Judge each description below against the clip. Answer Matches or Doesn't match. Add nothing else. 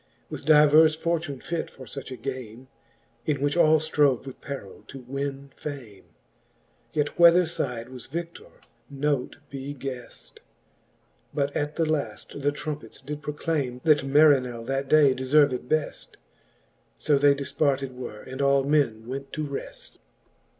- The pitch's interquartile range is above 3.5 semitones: Doesn't match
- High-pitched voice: Doesn't match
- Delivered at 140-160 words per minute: Matches